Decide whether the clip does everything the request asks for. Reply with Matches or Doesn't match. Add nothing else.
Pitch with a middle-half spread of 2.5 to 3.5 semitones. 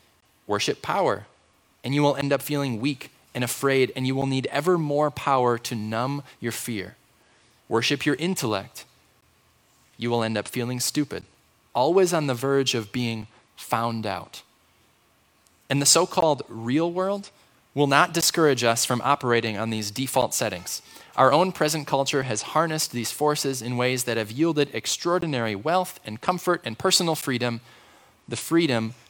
Doesn't match